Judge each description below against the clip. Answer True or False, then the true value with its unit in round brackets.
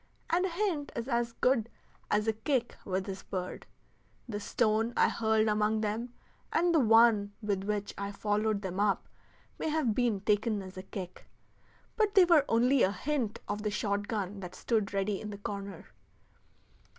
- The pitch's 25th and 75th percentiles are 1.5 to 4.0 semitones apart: True (2.9 semitones)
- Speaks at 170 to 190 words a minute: True (175 wpm)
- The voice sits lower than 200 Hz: False (215 Hz)